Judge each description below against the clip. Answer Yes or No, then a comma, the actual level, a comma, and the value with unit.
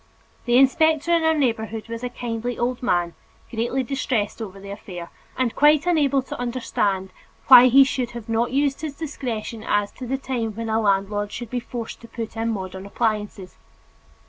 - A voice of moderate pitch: No, high, 235 Hz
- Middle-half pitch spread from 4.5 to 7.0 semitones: No, average, 3.8 semitones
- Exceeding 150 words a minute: Yes, average, 180 wpm